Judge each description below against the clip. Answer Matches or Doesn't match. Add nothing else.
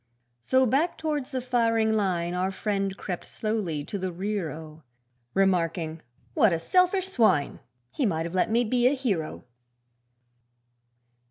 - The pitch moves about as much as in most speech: Doesn't match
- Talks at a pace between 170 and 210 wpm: Doesn't match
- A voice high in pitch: Matches